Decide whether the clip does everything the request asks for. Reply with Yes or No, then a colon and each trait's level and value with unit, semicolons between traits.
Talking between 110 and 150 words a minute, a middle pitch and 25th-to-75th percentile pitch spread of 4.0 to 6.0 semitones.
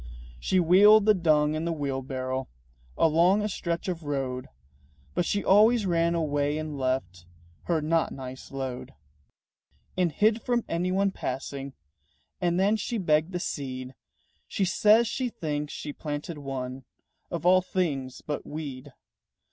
Yes: average, 140 wpm; medium, 155 Hz; average, 5.2 semitones